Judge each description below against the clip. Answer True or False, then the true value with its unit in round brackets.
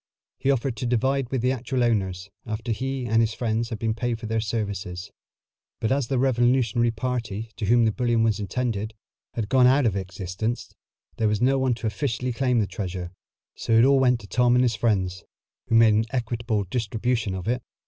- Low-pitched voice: True (115 Hz)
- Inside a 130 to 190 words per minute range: False (200 wpm)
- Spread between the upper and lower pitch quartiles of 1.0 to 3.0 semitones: True (2.7 semitones)